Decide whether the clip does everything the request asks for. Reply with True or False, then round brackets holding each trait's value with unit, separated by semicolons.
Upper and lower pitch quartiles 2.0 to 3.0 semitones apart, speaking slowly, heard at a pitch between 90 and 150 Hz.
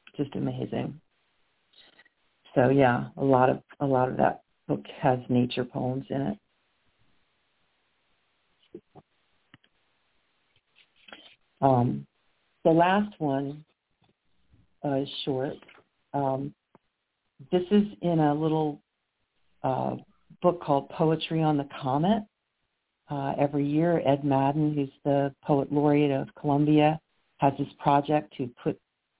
True (2.4 semitones; 110 wpm; 140 Hz)